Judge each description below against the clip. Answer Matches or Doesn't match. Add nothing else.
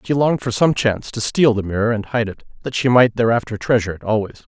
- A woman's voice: Doesn't match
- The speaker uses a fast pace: Matches